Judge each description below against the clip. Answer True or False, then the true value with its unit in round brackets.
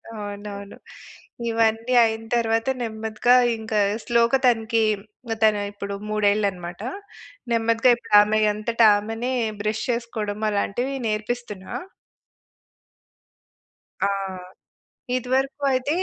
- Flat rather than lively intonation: True (2.1 semitones)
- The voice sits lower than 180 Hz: False (225 Hz)